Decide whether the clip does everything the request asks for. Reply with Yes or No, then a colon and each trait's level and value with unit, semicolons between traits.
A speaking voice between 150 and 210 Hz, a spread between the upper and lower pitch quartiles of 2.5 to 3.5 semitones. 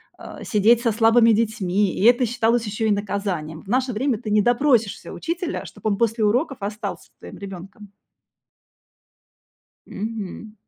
No: high, 220 Hz; average, 2.9 semitones